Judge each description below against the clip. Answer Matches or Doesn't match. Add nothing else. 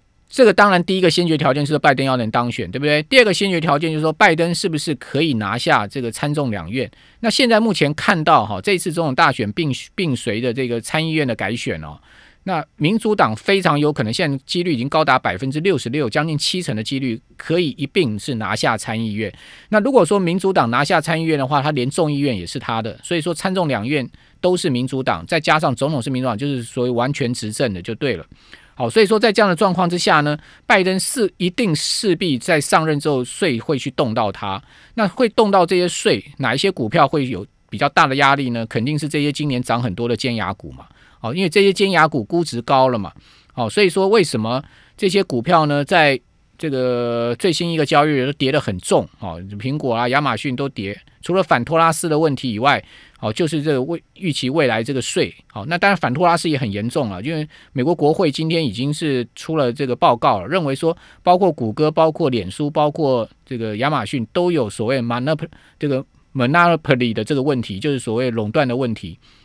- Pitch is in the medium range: Matches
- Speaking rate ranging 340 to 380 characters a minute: Matches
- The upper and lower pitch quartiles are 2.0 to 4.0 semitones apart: Doesn't match